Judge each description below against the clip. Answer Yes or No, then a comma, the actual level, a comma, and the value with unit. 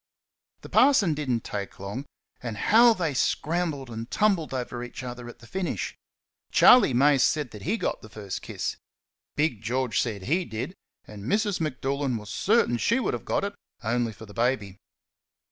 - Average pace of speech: Yes, average, 180 wpm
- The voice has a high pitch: No, low, 130 Hz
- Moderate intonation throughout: No, wide, 6.6 semitones